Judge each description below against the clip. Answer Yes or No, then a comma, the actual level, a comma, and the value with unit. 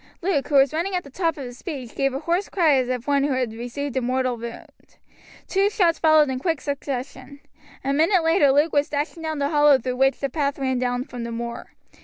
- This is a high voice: Yes, very high, 280 Hz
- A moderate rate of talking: No, fast, 235 wpm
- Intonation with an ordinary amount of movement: Yes, average, 3.5 semitones